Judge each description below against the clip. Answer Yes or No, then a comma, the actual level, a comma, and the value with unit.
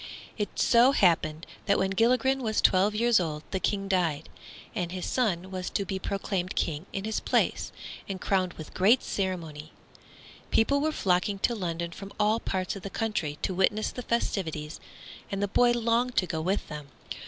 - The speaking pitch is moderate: No, high, 195 Hz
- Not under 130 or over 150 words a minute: No, average, 180 wpm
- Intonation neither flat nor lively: Yes, average, 3.8 semitones